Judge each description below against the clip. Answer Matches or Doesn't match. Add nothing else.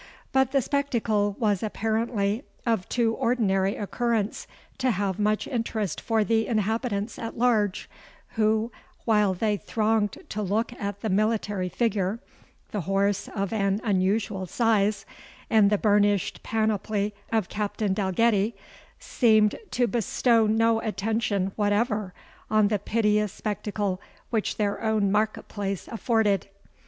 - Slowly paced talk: Matches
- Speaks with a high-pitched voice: Matches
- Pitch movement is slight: Matches